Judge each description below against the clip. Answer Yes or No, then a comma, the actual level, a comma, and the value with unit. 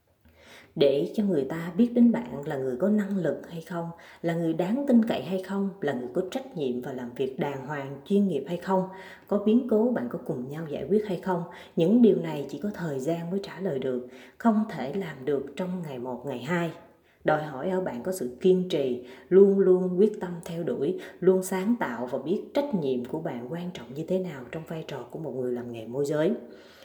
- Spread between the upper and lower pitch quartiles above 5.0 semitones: Yes, wide, 5.4 semitones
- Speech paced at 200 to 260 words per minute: Yes, average, 230 wpm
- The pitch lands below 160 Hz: No, medium, 180 Hz